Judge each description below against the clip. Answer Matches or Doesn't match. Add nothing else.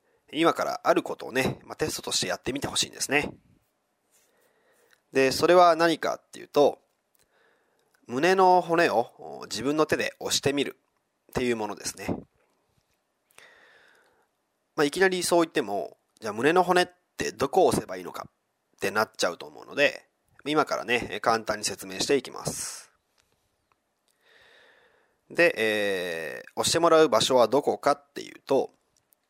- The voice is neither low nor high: Matches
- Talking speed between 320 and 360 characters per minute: Doesn't match